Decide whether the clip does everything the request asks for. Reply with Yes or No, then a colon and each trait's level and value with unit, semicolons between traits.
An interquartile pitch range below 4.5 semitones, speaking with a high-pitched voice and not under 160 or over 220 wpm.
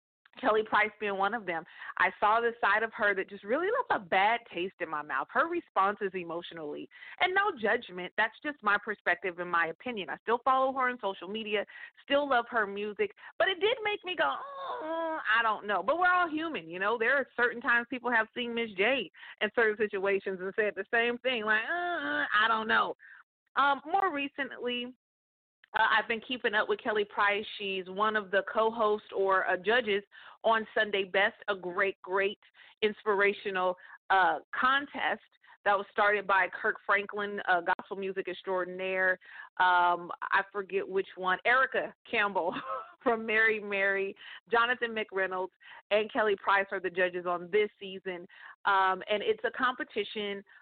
Yes: average, 4.0 semitones; high, 210 Hz; average, 175 wpm